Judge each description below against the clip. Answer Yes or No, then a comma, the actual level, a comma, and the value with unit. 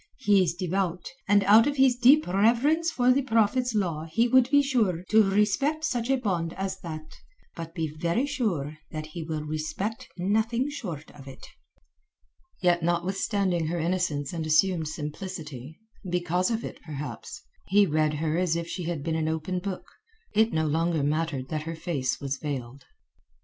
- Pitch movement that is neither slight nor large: No, wide, 5.8 semitones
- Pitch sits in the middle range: Yes, medium, 175 Hz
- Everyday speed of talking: Yes, average, 165 wpm